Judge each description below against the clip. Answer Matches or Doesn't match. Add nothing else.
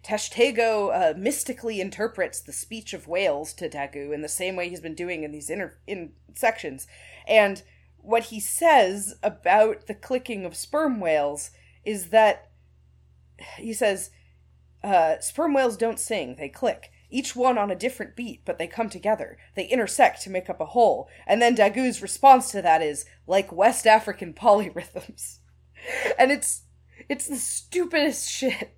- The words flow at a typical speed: Matches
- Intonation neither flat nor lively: Doesn't match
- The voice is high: Matches